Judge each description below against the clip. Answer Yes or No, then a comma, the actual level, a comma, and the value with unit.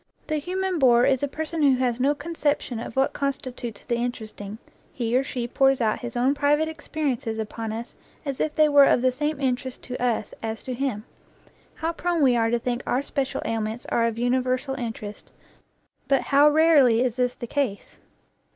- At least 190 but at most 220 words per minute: Yes, average, 195 wpm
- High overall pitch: Yes, very high, 255 Hz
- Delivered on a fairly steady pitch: No, average, 3.4 semitones